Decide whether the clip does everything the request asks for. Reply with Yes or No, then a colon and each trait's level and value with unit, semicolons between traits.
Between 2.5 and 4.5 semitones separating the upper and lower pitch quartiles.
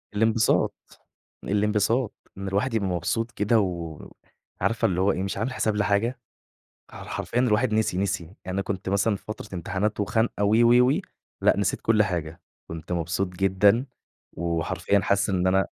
Yes: average, 2.8 semitones